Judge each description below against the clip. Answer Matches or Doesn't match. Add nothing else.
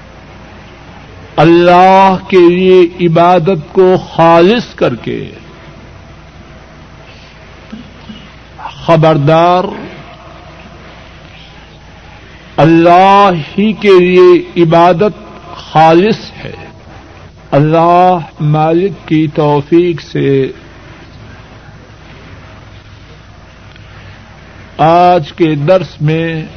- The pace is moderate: Doesn't match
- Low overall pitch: Doesn't match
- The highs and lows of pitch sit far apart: Matches